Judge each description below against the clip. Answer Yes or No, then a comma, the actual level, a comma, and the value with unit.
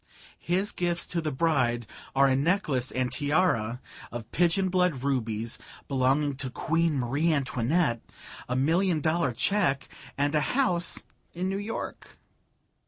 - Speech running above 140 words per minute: No, slow, 135 wpm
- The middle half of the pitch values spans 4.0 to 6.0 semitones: Yes, average, 5.2 semitones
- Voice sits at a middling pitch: Yes, medium, 145 Hz